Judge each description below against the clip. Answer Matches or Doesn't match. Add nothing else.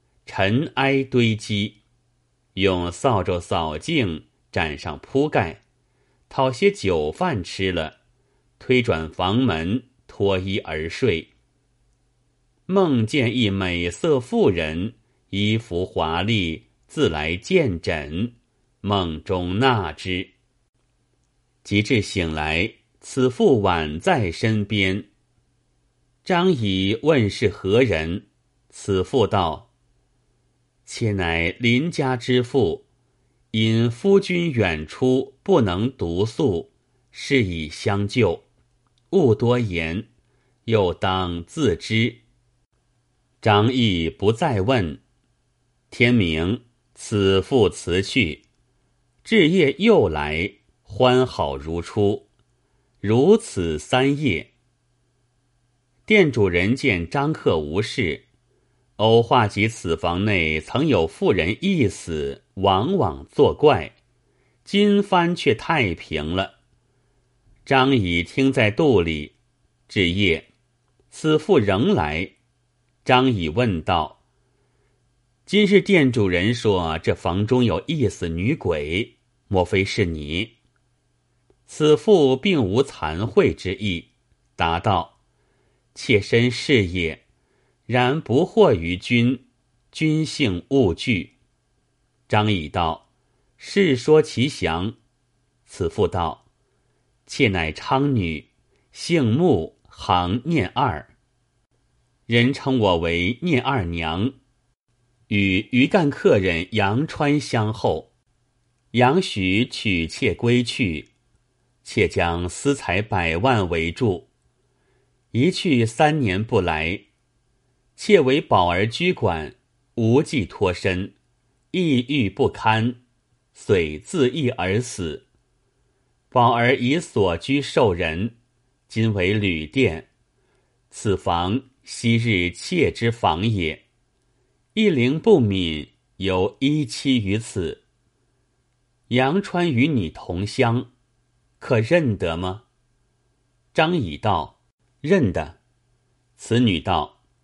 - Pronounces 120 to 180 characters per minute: Matches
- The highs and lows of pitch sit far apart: Doesn't match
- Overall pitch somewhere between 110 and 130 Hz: Matches